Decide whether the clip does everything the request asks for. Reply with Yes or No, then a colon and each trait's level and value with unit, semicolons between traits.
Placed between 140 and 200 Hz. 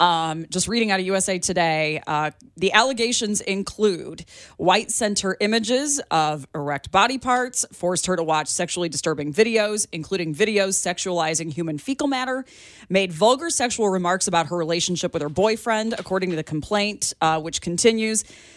Yes: high, 190 Hz